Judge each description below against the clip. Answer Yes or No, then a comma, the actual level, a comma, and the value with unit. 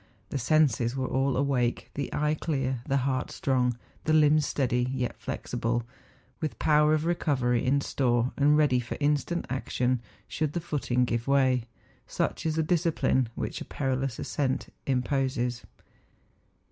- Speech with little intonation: No, average, 3.1 semitones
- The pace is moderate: Yes, average, 145 wpm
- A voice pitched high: No, low, 135 Hz